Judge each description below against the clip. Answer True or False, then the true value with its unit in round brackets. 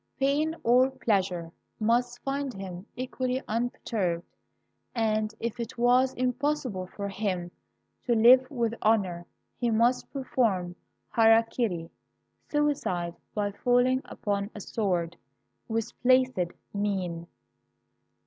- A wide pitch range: False (4.7 semitones)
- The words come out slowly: True (110 wpm)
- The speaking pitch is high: True (225 Hz)